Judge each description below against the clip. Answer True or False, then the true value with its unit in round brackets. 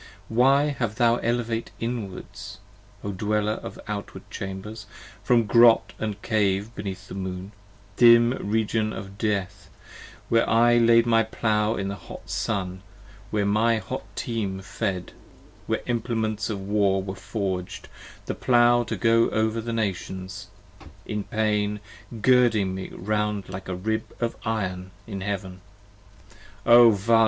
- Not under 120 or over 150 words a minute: True (140 wpm)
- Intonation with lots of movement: False (2.8 semitones)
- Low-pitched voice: True (105 Hz)